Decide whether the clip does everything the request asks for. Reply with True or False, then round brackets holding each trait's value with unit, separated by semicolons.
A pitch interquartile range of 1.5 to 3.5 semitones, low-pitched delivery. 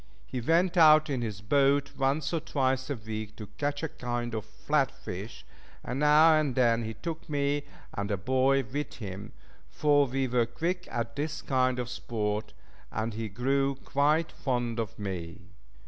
False (4.3 semitones; 130 Hz)